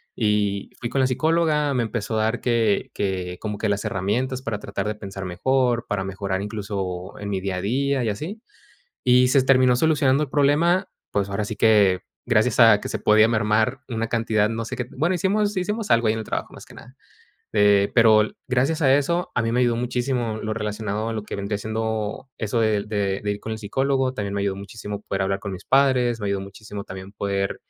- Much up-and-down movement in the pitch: No, average, 4.1 semitones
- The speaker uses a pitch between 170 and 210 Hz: No, low, 110 Hz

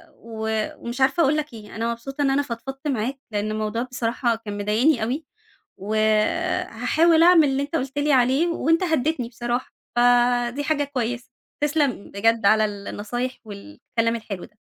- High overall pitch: Yes, high, 245 Hz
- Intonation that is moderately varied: Yes, average, 4.2 semitones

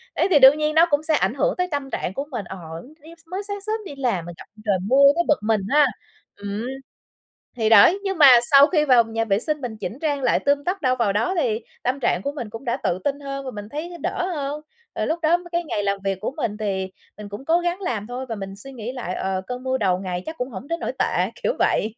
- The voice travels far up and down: Yes, wide, 6.4 semitones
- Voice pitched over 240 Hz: Yes, very high, 260 Hz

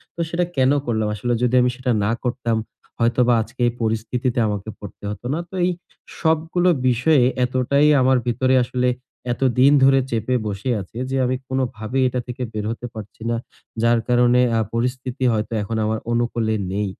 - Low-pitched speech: Yes, low, 125 Hz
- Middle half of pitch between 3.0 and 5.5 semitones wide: No, narrow, 2.4 semitones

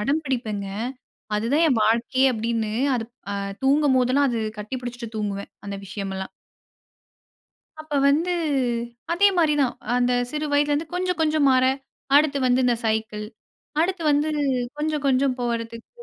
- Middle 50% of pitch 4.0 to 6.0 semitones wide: Yes, average, 4.7 semitones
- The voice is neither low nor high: No, very high, 255 Hz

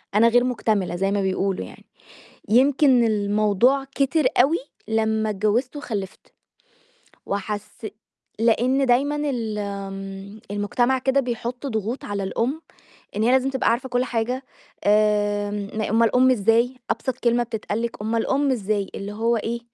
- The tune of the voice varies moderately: Yes, average, 3.6 semitones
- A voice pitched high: Yes, high, 225 Hz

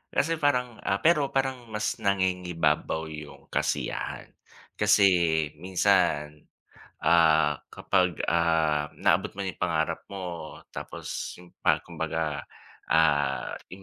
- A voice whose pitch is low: Yes, very low, 85 Hz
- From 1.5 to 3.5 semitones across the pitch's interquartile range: No, average, 3.9 semitones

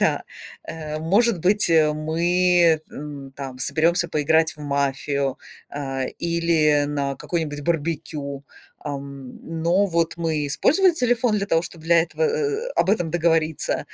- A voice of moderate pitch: Yes, medium, 160 Hz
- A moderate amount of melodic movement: Yes, average, 3.1 semitones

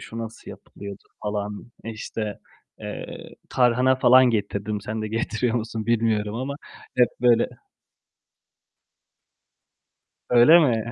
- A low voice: Yes, low, 115 Hz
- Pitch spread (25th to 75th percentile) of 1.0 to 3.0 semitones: Yes, narrow, 2.4 semitones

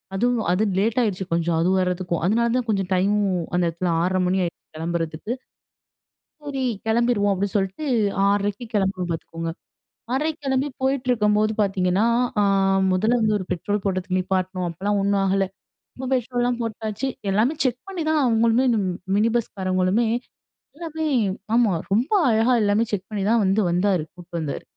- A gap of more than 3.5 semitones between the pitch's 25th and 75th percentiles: Yes, average, 4.2 semitones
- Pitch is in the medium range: No, high, 205 Hz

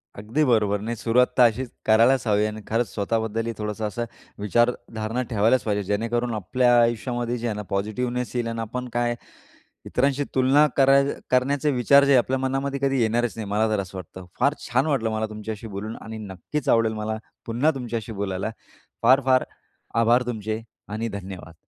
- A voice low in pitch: Yes, low, 115 Hz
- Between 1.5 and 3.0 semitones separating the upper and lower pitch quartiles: Yes, average, 2.7 semitones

